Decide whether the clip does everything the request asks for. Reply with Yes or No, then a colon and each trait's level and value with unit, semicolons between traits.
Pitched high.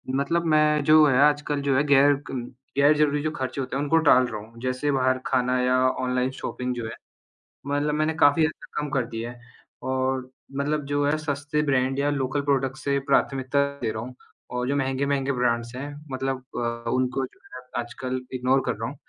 No: low, 135 Hz